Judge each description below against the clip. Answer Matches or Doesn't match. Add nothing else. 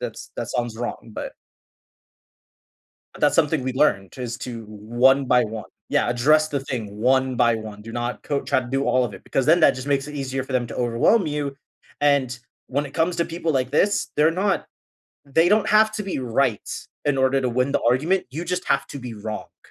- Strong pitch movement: Doesn't match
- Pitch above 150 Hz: Doesn't match